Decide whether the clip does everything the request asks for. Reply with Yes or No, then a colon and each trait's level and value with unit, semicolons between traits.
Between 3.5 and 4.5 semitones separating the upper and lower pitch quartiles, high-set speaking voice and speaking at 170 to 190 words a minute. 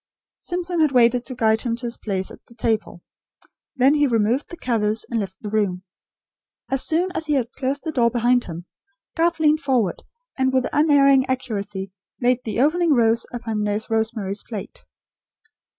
Yes: average, 4.1 semitones; high, 240 Hz; average, 175 wpm